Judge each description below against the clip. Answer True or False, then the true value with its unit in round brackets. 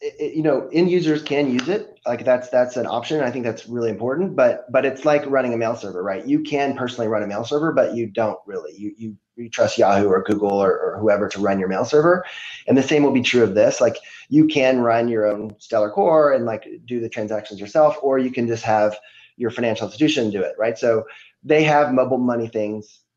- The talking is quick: True (240 wpm)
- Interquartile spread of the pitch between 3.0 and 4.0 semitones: False (5.1 semitones)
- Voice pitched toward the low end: True (120 Hz)